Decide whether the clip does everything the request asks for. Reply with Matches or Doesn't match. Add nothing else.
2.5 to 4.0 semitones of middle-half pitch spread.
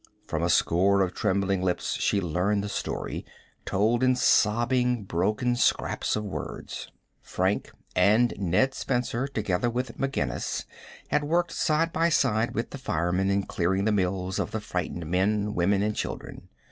Doesn't match